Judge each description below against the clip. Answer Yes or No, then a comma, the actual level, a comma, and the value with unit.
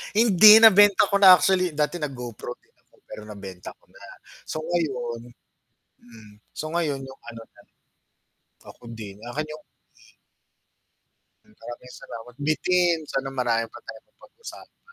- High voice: No, medium, 140 Hz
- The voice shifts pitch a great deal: Yes, wide, 7.1 semitones